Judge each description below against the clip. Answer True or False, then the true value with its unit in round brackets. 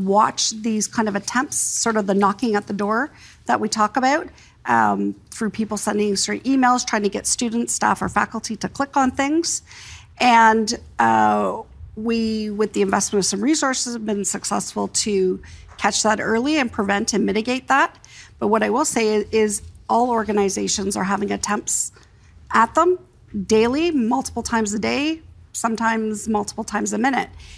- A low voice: False (220 Hz)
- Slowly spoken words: False (170 wpm)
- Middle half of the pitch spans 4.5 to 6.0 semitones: False (3.0 semitones)